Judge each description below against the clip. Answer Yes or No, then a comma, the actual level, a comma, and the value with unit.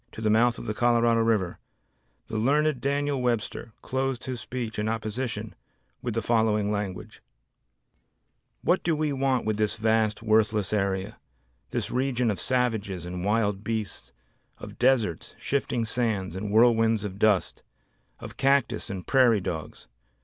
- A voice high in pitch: No, low, 115 Hz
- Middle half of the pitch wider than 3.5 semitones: No, average, 3.0 semitones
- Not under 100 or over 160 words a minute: Yes, average, 145 wpm